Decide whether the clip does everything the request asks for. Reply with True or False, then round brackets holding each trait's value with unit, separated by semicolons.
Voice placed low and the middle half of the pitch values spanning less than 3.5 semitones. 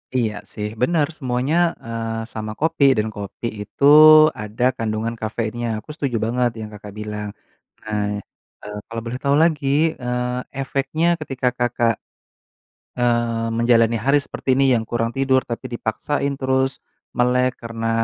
True (120 Hz; 2.8 semitones)